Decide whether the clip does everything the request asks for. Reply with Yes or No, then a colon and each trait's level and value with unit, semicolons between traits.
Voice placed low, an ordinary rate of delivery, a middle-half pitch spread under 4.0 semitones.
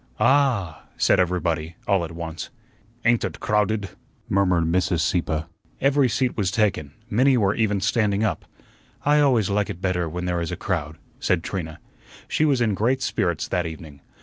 No: very low, 95 Hz; average, 170 wpm; average, 4.8 semitones